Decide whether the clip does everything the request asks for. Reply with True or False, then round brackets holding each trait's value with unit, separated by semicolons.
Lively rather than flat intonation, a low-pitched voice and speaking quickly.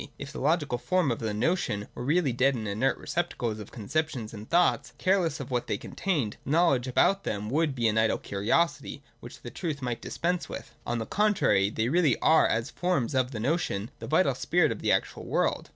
True (6.5 semitones; 130 Hz; 210 wpm)